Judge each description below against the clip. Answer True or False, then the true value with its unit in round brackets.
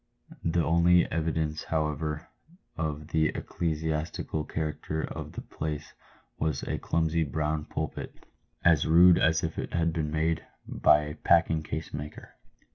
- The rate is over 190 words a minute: False (135 wpm)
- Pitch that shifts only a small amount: True (1.3 semitones)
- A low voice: True (80 Hz)